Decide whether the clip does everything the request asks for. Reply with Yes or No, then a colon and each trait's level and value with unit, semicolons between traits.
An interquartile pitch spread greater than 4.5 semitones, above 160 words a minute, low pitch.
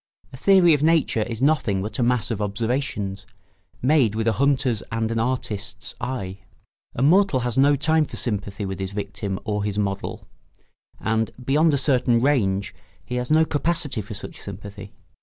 Yes: wide, 5.4 semitones; average, 175 wpm; low, 115 Hz